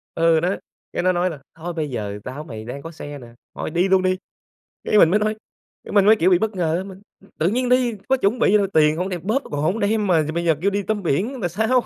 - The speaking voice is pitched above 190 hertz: No, medium, 185 Hz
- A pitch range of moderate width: Yes, average, 4.7 semitones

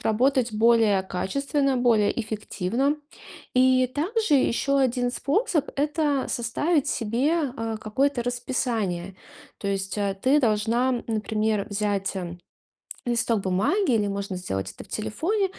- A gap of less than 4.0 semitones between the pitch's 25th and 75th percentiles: No, average, 4.9 semitones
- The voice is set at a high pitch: Yes, high, 235 Hz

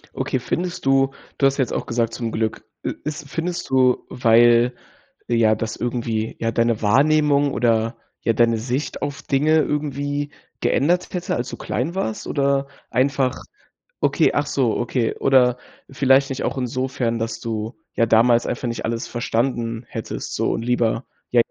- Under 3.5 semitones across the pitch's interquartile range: Yes, average, 3.1 semitones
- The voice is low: Yes, low, 125 Hz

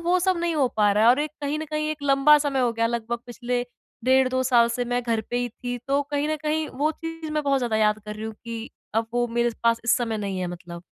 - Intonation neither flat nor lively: Yes, average, 4.3 semitones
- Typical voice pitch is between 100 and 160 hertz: No, high, 245 Hz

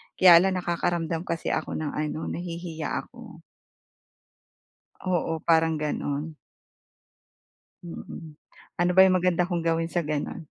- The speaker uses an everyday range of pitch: No, narrow, 1.6 semitones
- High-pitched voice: No, medium, 165 Hz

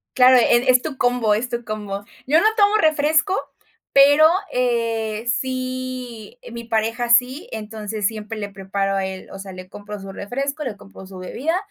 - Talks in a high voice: Yes, high, 235 Hz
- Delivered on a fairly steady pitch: No, average, 3.7 semitones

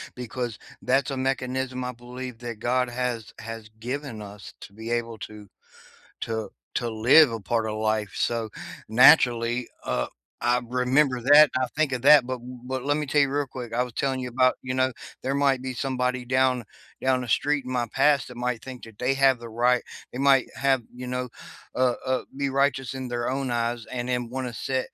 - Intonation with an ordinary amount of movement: No, narrow, 1.9 semitones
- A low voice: Yes, low, 125 Hz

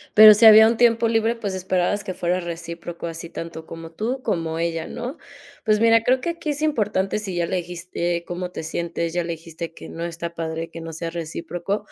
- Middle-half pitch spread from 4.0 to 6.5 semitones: Yes, average, 4.4 semitones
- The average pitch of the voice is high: No, medium, 175 Hz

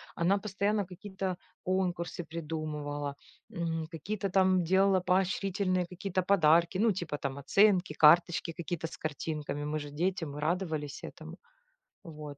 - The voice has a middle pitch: Yes, medium, 175 Hz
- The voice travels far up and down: No, average, 3.7 semitones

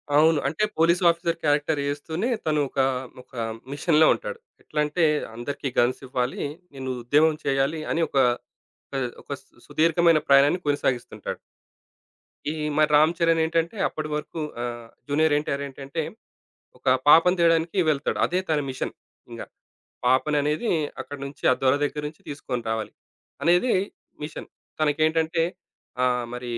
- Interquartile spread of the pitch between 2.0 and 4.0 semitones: Yes, average, 2.8 semitones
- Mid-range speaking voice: Yes, medium, 150 Hz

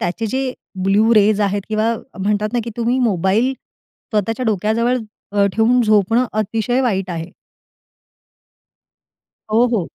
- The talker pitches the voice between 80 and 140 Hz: No, high, 215 Hz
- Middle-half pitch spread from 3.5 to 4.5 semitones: No, average, 2.7 semitones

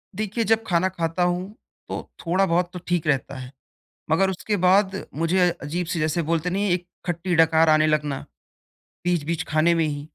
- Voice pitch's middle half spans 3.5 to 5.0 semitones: No, average, 2.8 semitones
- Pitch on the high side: No, medium, 170 Hz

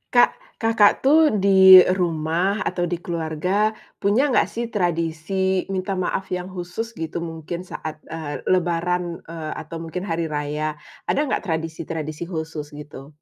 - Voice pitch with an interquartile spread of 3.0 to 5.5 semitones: No, narrow, 2.4 semitones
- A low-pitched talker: No, medium, 165 Hz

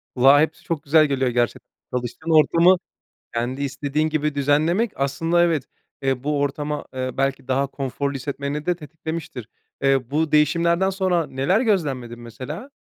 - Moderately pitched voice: Yes, medium, 145 Hz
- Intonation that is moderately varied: Yes, average, 3.4 semitones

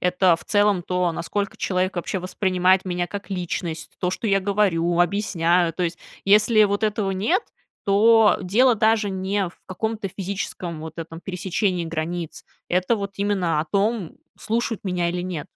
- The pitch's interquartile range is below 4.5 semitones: Yes, narrow, 2.6 semitones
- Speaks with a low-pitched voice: No, high, 190 Hz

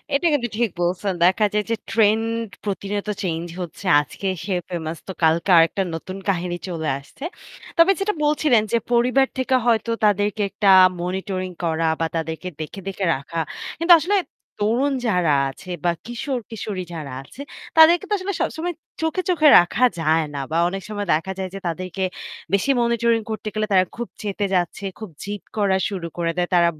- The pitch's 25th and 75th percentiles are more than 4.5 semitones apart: Yes, average, 5.2 semitones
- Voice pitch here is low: No, high, 200 Hz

